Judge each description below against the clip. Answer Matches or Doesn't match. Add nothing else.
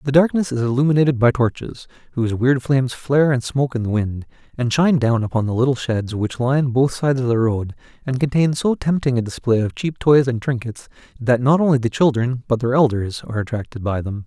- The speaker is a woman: Doesn't match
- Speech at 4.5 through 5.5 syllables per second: Doesn't match